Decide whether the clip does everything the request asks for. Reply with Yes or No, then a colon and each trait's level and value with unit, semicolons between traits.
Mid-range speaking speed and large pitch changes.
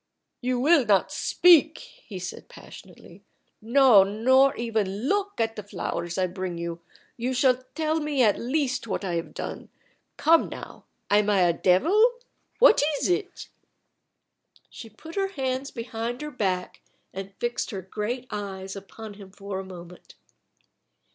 Yes: average, 150 wpm; wide, 6.1 semitones